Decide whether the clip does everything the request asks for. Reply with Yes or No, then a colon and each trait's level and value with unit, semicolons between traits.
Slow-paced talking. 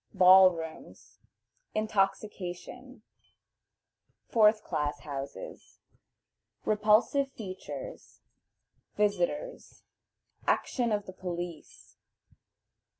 Yes: slow, 60 wpm